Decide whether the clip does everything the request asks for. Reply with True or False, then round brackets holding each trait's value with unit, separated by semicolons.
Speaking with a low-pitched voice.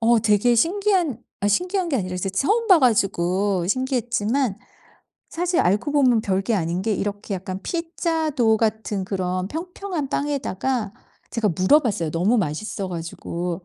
False (220 Hz)